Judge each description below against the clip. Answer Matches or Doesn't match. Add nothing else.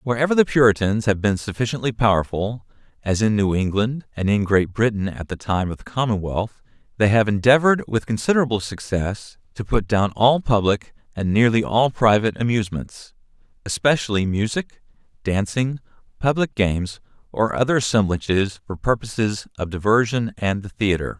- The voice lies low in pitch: Matches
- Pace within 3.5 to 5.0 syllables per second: Doesn't match